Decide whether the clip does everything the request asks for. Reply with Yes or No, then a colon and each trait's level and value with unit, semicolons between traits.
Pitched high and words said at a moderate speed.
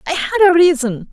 No: very high, 320 Hz; fast, 215 wpm